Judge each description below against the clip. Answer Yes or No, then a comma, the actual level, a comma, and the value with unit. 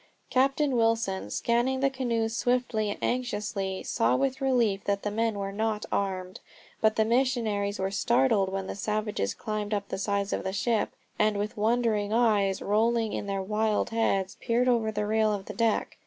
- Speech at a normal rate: Yes, average, 180 wpm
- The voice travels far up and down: No, average, 2.7 semitones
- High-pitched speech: Yes, high, 215 Hz